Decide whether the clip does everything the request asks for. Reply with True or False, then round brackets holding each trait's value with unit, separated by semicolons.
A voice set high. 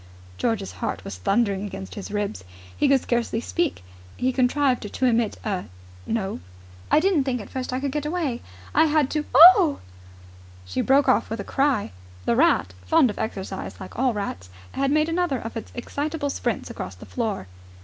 True (245 Hz)